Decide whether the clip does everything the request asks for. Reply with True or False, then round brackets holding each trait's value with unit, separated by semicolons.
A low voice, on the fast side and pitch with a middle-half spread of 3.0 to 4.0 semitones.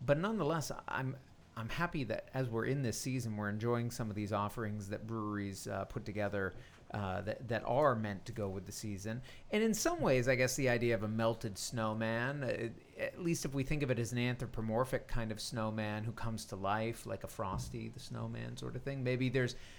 True (115 Hz; 220 wpm; 3.6 semitones)